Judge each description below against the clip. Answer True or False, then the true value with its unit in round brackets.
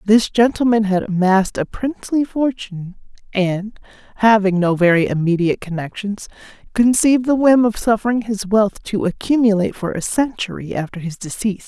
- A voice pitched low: False (210 Hz)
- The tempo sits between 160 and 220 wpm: False (145 wpm)